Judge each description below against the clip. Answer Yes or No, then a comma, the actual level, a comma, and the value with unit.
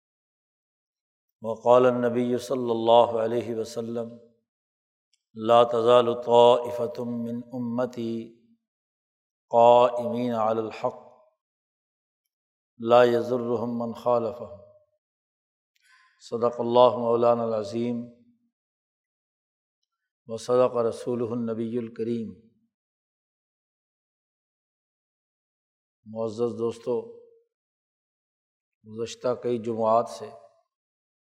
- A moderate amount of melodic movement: No, narrow, 1.2 semitones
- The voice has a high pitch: No, low, 120 Hz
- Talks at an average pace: No, slow, 55 wpm